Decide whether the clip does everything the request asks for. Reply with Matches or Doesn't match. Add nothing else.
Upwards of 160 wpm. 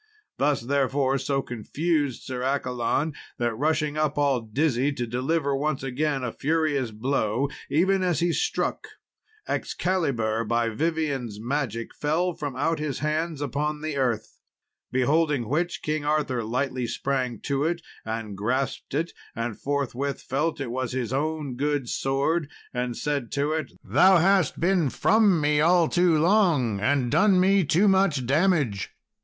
Doesn't match